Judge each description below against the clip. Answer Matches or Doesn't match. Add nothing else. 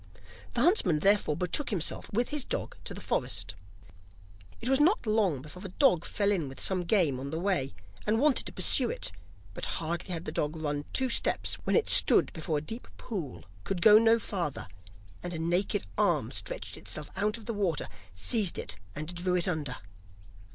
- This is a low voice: Doesn't match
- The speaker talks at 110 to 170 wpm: Doesn't match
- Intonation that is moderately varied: Doesn't match